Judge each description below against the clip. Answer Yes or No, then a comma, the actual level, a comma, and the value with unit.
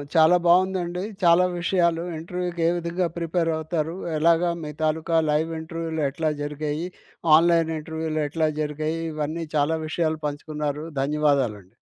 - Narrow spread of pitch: Yes, narrow, 1.9 semitones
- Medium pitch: Yes, medium, 160 Hz